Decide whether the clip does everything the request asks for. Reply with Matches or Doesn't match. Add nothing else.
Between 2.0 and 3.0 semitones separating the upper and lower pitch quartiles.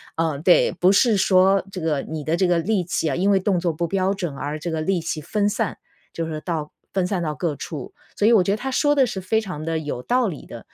Doesn't match